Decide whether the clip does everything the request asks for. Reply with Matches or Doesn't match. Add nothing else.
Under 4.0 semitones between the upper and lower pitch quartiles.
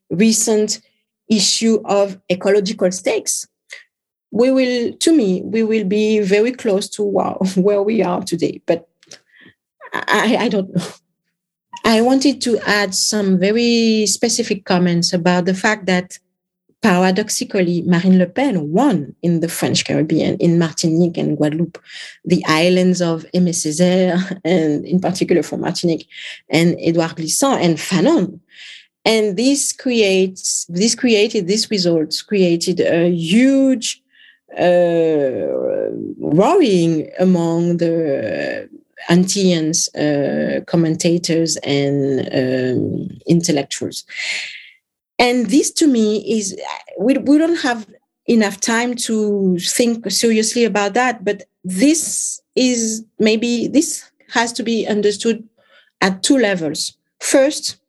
Doesn't match